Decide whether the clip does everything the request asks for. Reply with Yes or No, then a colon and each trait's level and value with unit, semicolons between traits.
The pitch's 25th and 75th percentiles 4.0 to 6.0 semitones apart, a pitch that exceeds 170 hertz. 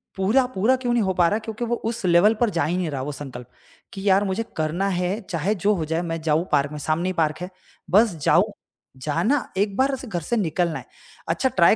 Yes: average, 4.9 semitones; medium, 185 Hz